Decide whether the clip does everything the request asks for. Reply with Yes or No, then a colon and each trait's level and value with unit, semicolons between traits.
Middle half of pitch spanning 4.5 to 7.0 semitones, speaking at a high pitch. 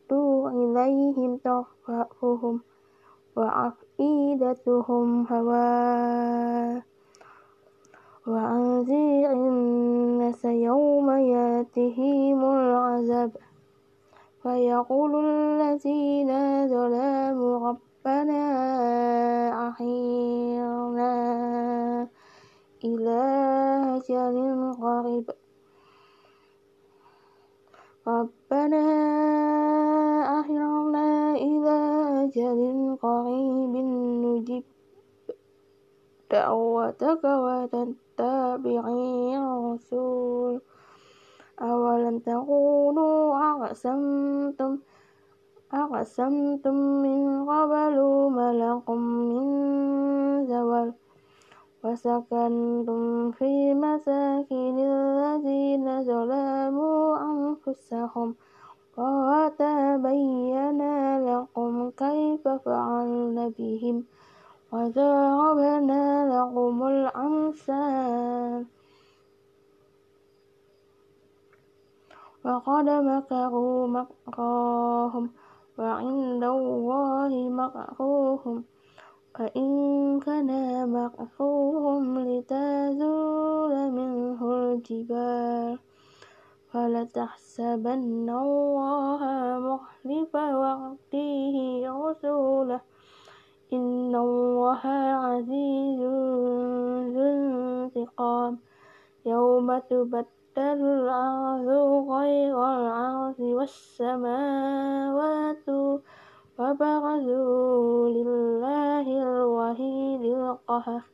No: average, 2.7 semitones; very high, 260 Hz